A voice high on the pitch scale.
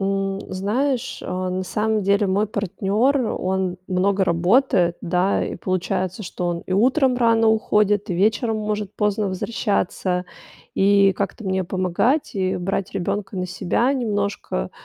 Yes: high, 195 Hz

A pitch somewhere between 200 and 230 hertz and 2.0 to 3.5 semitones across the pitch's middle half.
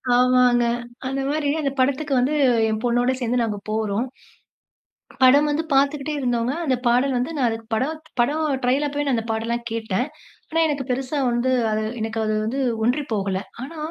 No: very high, 250 Hz; average, 3.2 semitones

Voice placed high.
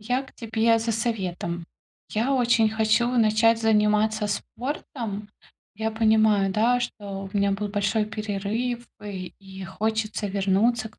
Yes: high, 215 Hz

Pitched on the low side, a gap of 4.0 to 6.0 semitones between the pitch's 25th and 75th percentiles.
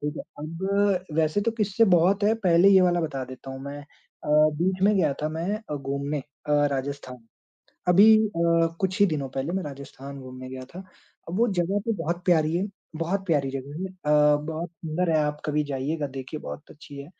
No: medium, 155 Hz; average, 4.7 semitones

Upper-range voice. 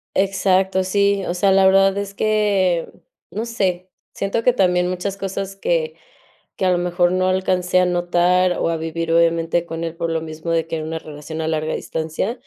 No: medium, 180 Hz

